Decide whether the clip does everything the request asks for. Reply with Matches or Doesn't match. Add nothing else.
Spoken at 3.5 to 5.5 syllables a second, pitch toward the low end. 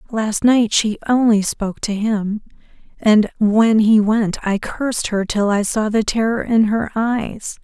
Doesn't match